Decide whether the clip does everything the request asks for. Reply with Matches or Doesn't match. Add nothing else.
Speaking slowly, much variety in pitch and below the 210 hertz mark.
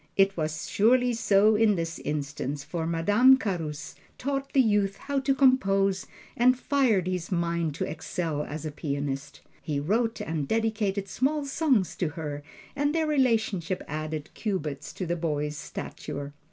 Doesn't match